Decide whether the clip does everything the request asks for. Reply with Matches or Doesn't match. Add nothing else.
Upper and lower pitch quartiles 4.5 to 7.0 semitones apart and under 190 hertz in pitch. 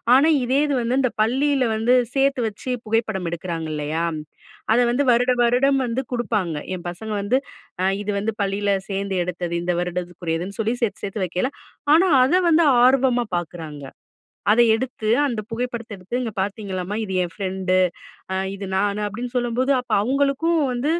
Doesn't match